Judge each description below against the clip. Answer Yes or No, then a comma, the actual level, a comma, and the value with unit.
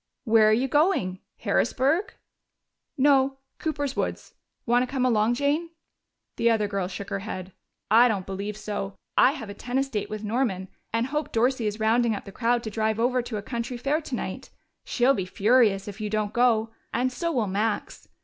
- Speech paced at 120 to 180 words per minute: No, average, 190 wpm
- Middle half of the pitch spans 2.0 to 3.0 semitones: No, average, 3.7 semitones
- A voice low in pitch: No, high, 230 Hz